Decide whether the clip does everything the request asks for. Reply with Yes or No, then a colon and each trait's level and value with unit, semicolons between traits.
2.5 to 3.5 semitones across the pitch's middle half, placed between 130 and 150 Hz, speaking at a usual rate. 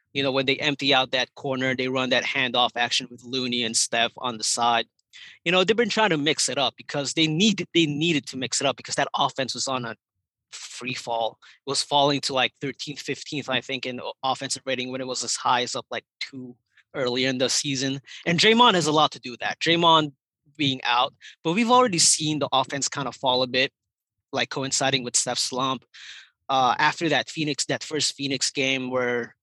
No: average, 2.8 semitones; low, 135 Hz; fast, 220 wpm